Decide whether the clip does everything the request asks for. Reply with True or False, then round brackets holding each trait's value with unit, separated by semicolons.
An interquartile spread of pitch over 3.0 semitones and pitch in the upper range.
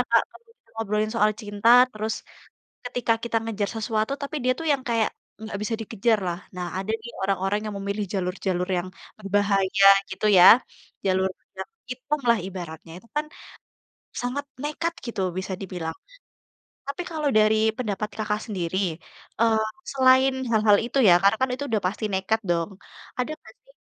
True (3.5 semitones; 215 Hz)